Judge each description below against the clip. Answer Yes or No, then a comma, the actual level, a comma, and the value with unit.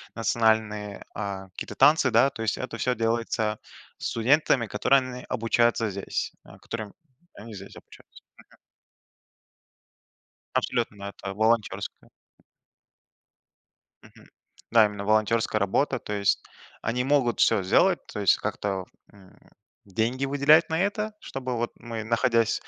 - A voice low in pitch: Yes, low, 115 Hz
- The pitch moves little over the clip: No, average, 3.4 semitones